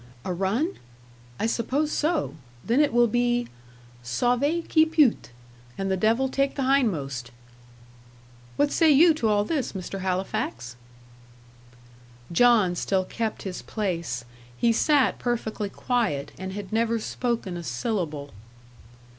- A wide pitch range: Yes, wide, 6.0 semitones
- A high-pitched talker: Yes, high, 225 Hz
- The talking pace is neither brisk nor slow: No, slow, 130 wpm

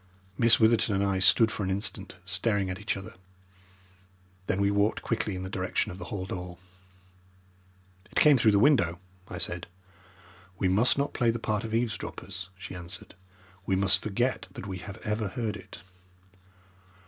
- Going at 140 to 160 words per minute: No, average, 170 wpm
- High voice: No, low, 100 Hz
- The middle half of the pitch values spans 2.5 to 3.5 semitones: Yes, average, 3.1 semitones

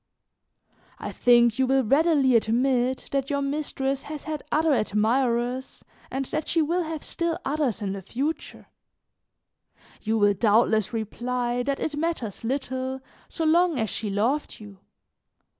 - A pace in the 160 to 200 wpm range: No, average, 140 wpm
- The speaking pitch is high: Yes, very high, 260 Hz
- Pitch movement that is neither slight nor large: Yes, average, 4.4 semitones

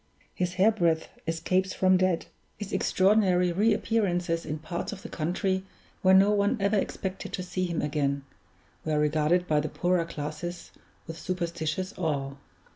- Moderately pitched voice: Yes, medium, 180 Hz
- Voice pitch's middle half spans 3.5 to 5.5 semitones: No, average, 2.9 semitones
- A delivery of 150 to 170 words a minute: Yes, average, 155 wpm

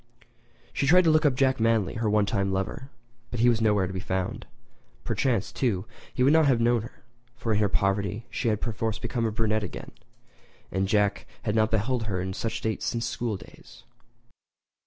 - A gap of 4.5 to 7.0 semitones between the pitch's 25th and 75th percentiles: No, average, 2.9 semitones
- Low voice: Yes, low, 110 Hz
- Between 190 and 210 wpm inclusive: Yes, average, 200 wpm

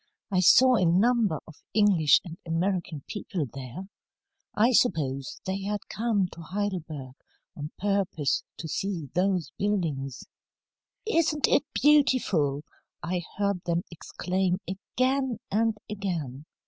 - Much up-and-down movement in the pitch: No, average, 4.6 semitones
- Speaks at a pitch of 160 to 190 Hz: Yes, medium, 185 Hz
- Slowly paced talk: Yes, slow, 120 wpm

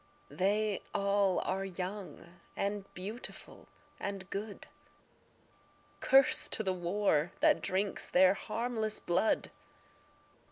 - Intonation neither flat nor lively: No, narrow, 2.3 semitones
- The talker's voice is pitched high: Yes, high, 200 Hz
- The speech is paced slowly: Yes, slow, 95 wpm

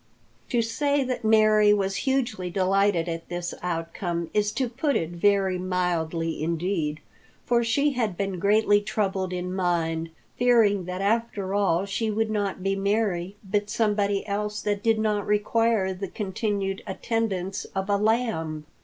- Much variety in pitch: No, average, 3.0 semitones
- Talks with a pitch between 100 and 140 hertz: No, high, 200 Hz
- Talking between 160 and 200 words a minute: No, average, 150 wpm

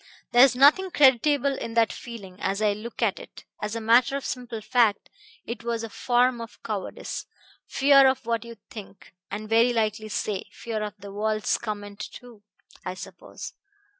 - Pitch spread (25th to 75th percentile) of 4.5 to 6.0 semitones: No, average, 2.7 semitones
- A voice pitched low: No, high, 230 Hz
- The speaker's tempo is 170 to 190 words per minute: Yes, average, 175 wpm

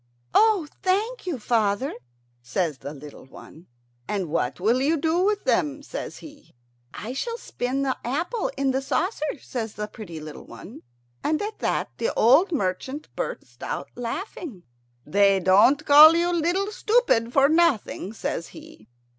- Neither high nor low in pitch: No, very high, 270 Hz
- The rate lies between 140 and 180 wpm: Yes, average, 155 wpm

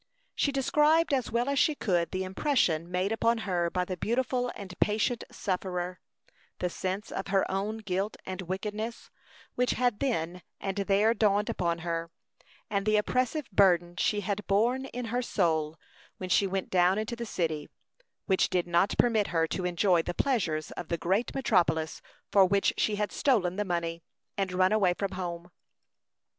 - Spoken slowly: No, average, 175 wpm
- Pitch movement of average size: Yes, average, 3.9 semitones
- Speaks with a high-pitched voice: Yes, high, 195 Hz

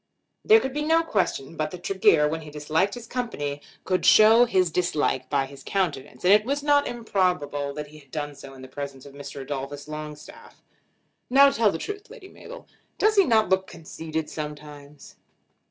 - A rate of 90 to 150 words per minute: No, average, 185 wpm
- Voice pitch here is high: No, medium, 160 Hz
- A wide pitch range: Yes, wide, 7.9 semitones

